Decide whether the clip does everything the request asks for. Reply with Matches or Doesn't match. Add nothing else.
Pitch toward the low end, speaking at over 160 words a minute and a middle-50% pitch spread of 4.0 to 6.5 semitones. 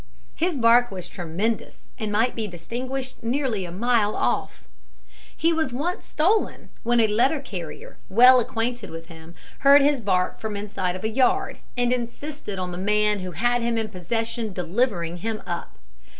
Doesn't match